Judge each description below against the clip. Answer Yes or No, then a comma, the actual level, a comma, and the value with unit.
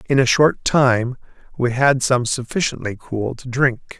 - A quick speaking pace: No, average, 165 wpm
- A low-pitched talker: Yes, low, 125 Hz